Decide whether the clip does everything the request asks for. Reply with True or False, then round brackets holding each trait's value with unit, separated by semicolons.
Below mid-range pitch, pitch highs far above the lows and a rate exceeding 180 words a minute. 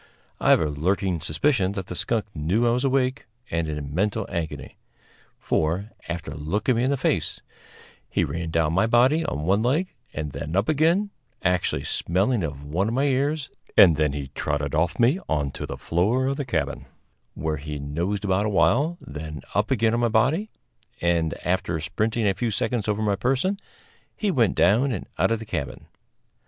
True (100 Hz; 7.5 semitones; 190 wpm)